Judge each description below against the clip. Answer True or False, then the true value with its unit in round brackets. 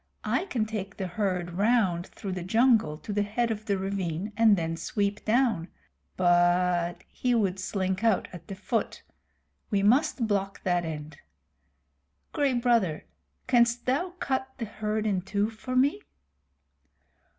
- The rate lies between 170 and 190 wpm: False (150 wpm)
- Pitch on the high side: True (205 Hz)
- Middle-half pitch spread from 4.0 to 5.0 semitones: True (4.3 semitones)